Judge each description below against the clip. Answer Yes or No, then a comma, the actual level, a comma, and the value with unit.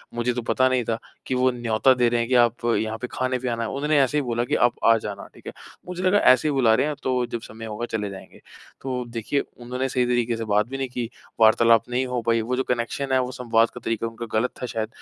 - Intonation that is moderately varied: No, narrow, 2.0 semitones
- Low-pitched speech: Yes, low, 120 Hz